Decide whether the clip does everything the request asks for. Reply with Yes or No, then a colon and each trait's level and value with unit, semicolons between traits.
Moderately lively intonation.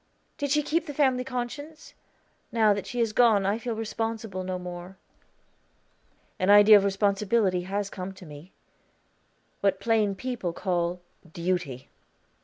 Yes: average, 4.0 semitones